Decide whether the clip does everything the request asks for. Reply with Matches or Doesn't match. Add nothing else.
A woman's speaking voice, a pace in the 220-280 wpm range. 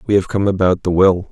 Doesn't match